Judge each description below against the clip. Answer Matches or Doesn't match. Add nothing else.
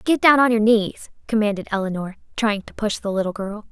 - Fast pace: Matches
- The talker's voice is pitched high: Matches